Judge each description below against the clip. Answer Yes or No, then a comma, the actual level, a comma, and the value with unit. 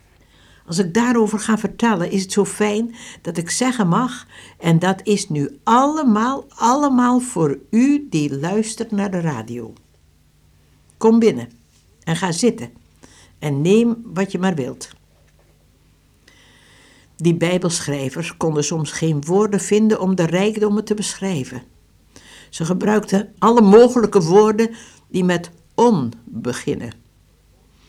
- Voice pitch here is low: No, medium, 180 Hz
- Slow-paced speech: Yes, slow, 125 wpm